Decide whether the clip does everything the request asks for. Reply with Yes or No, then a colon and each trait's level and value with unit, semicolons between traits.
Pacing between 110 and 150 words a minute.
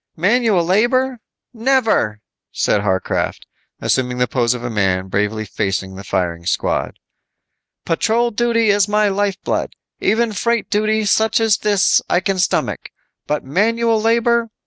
Yes: slow, 135 wpm